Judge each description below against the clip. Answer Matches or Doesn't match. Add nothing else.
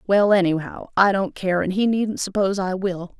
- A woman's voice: Matches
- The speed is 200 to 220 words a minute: Matches